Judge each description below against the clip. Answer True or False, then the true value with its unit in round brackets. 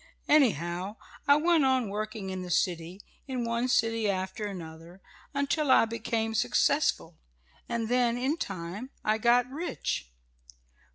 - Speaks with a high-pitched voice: True (225 Hz)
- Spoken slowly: True (130 wpm)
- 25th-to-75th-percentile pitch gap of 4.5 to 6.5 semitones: True (5.1 semitones)